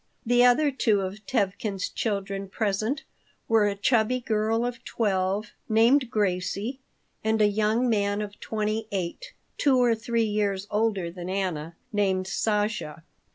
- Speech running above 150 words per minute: No, average, 140 wpm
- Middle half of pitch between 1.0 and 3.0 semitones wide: Yes, narrow, 2.6 semitones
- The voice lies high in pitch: Yes, high, 210 Hz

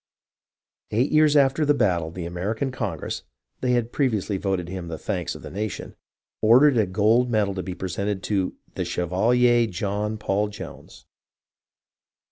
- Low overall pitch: Yes, low, 105 Hz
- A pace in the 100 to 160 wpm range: Yes, average, 155 wpm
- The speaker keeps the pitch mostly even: No, average, 4.6 semitones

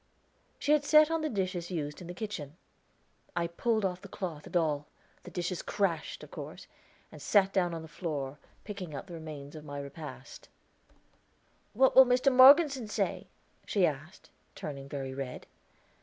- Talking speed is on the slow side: No, average, 165 wpm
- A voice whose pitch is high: No, medium, 175 Hz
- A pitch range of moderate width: No, wide, 5.9 semitones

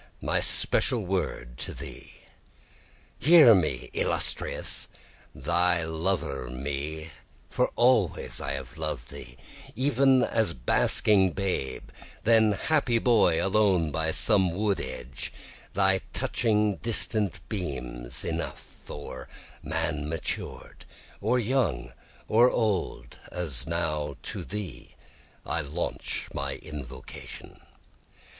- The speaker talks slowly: Yes, slow, 105 wpm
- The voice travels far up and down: Yes, wide, 7.1 semitones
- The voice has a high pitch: No, very low, 85 Hz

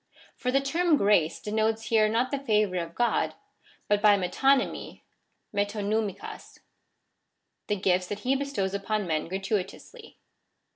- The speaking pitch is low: No, high, 210 Hz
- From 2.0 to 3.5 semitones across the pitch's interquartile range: No, average, 4.5 semitones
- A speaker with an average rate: No, slow, 130 wpm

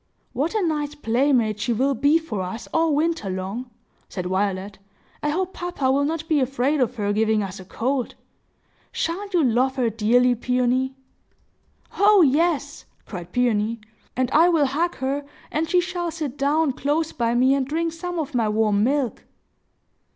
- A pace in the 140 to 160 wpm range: No, average, 170 wpm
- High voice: Yes, very high, 265 Hz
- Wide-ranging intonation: Yes, wide, 5.7 semitones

